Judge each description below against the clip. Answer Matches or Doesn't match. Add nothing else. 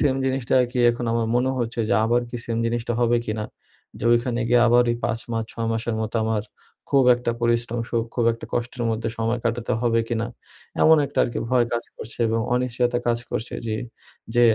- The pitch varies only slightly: Matches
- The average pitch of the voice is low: Matches